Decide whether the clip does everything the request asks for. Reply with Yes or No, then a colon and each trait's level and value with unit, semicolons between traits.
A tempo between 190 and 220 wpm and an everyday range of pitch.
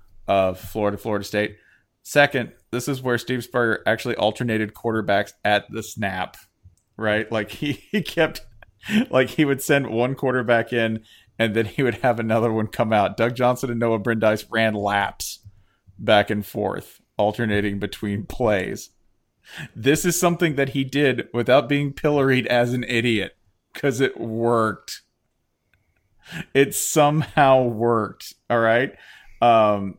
No: average, 140 wpm; average, 3.9 semitones